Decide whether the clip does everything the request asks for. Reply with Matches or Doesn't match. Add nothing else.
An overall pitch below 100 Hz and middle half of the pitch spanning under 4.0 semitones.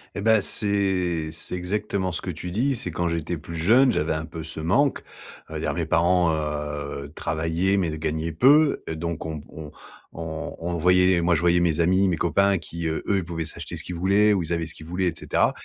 Matches